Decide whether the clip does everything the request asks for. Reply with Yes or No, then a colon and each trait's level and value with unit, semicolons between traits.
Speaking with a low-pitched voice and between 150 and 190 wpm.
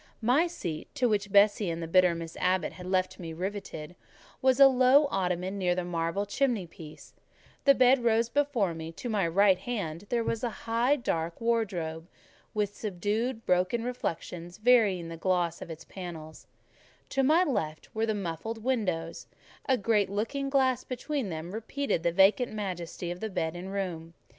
No: high, 200 Hz; average, 170 wpm